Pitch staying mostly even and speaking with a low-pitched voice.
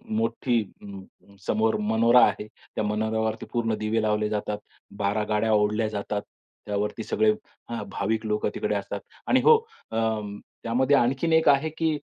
Yes: narrow, 2.1 semitones; low, 110 Hz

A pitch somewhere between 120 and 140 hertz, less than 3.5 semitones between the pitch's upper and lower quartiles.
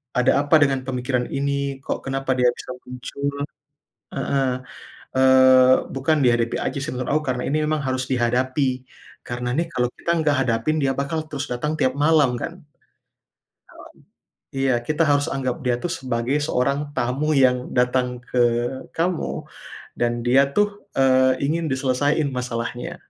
Yes: low, 135 Hz; narrow, 2.5 semitones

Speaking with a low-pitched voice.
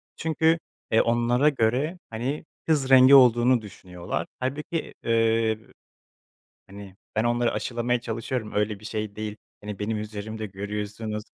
Yes: low, 115 Hz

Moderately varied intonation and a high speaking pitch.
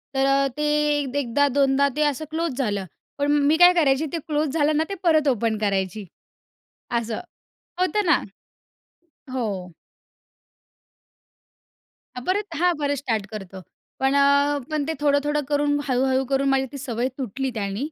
Yes: average, 3.4 semitones; very high, 280 Hz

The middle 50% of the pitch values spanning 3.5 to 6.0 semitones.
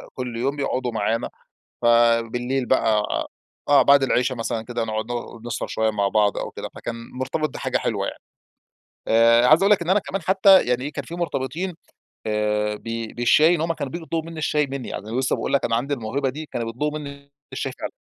Yes: average, 4.6 semitones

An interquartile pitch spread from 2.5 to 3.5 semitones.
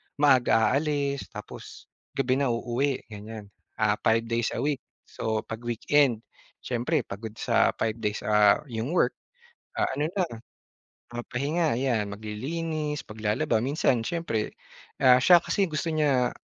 No: average, 4.7 semitones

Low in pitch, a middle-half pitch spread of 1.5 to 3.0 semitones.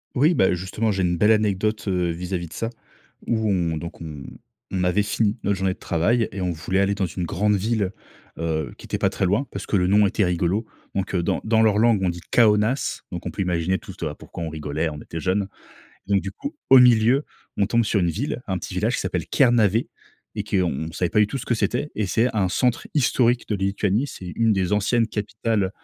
No: low, 100 Hz; average, 3.6 semitones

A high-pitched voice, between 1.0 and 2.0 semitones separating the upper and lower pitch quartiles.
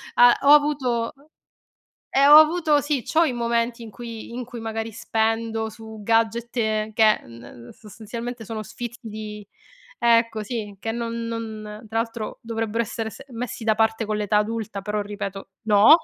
Yes: high, 225 Hz; narrow, 1.7 semitones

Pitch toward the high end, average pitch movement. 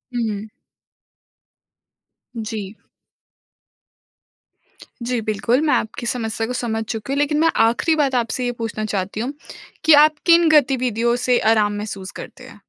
Yes: high, 235 Hz; average, 3.6 semitones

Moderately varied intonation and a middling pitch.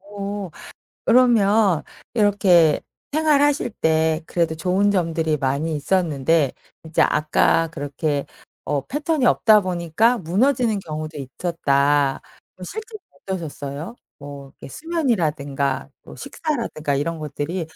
No: wide, 6.0 semitones; medium, 170 Hz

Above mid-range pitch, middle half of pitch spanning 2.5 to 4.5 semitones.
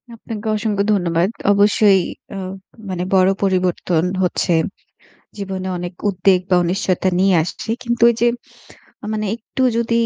Yes: high, 195 Hz; average, 2.8 semitones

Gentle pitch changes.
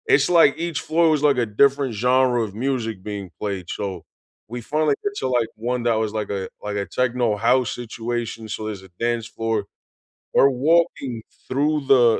No: average, 3.6 semitones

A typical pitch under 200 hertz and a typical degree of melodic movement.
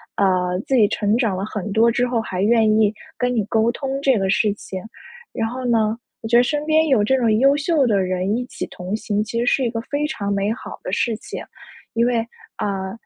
No: high, 225 Hz; average, 3.6 semitones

